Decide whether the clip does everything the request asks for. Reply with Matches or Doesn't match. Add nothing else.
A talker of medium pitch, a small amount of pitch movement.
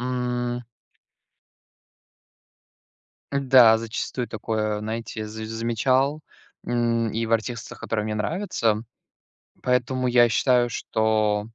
Doesn't match